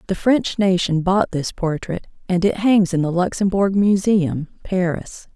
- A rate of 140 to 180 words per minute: Yes, average, 155 wpm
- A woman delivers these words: Yes, female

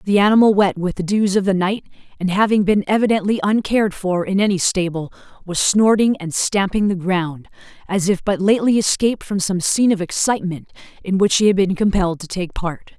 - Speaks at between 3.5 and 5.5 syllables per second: No, 5.7 syllables/s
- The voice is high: Yes, high, 195 Hz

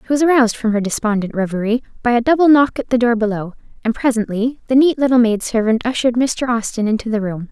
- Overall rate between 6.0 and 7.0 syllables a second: Yes, 6.5 syllables/s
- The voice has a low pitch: No, high, 235 Hz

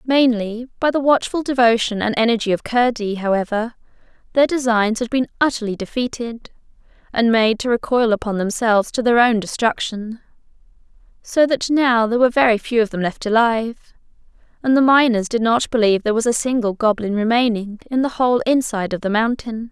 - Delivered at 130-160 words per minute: No, average, 170 wpm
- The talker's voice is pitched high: Yes, high, 230 Hz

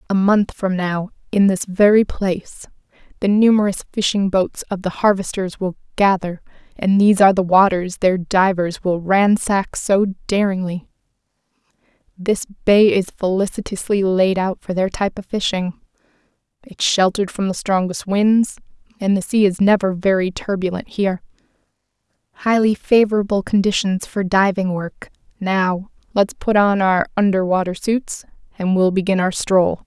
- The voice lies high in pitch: Yes, high, 195 Hz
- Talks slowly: No, average, 145 wpm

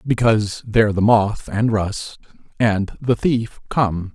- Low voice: Yes, low, 110 Hz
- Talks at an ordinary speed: Yes, average, 145 wpm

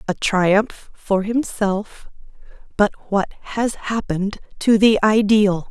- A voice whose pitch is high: Yes, high, 205 Hz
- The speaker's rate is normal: No, slow, 115 wpm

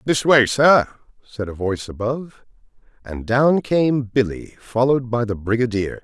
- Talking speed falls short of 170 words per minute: Yes, average, 150 wpm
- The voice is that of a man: Yes, male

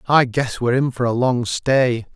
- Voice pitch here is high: No, low, 125 Hz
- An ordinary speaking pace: No, fast, 225 wpm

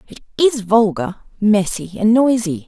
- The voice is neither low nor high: No, high, 210 Hz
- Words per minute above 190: No, slow, 135 wpm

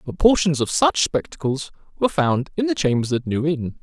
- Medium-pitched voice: Yes, medium, 155 Hz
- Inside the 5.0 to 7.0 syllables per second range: Yes, 5.3 syllables/s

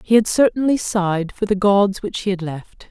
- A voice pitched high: Yes, high, 200 Hz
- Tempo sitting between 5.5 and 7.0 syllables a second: No, 5.0 syllables/s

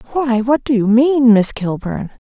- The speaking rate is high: No, average, 185 wpm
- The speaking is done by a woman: Yes, female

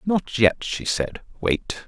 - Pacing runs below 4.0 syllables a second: Yes, 3.1 syllables/s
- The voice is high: No, low, 130 Hz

